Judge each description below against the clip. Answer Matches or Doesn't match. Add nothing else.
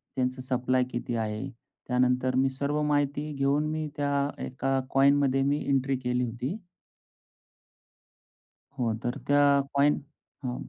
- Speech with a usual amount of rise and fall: Doesn't match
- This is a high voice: Doesn't match